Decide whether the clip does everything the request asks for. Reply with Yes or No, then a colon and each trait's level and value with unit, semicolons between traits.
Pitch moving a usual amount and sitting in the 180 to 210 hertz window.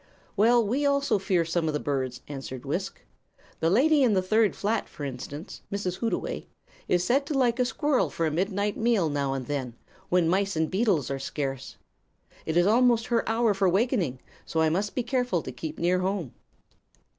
No: wide, 6.7 semitones; high, 190 Hz